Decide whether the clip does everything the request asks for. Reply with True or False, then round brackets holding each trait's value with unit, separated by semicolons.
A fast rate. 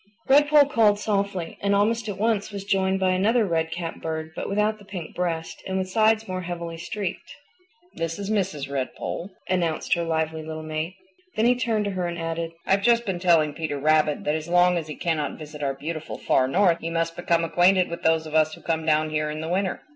True (220 wpm)